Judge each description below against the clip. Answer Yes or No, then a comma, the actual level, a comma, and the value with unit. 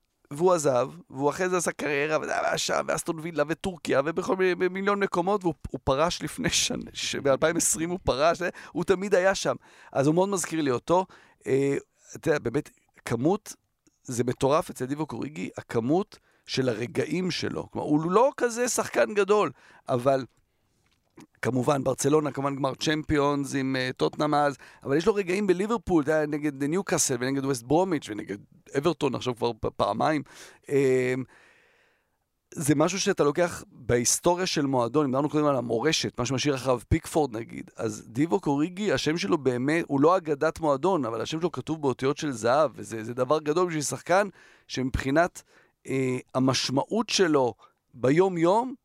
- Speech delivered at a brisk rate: Yes, fast, 155 wpm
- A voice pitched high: No, medium, 150 Hz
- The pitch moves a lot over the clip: No, average, 4.9 semitones